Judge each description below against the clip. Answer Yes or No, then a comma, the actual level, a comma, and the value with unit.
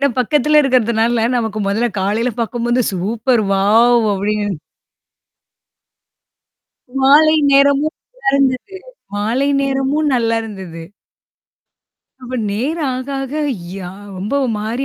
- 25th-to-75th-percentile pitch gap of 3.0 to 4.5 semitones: Yes, average, 4.2 semitones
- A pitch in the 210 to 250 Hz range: Yes, high, 240 Hz